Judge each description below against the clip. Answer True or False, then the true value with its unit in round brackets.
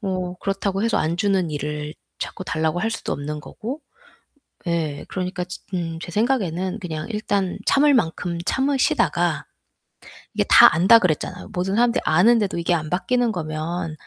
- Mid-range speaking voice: True (180 Hz)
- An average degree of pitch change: True (4.5 semitones)